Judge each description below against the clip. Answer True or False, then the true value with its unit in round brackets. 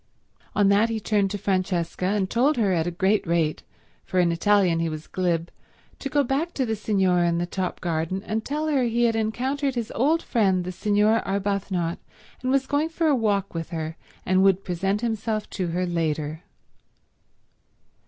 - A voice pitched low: False (200 Hz)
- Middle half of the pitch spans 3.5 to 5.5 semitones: True (4.5 semitones)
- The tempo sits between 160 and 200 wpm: True (185 wpm)